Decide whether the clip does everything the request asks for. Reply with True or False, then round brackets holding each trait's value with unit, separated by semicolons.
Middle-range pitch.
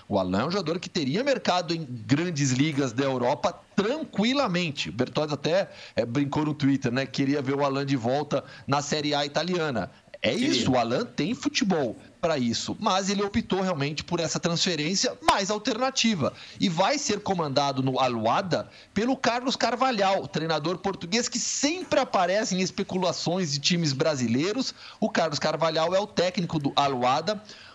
True (170 Hz)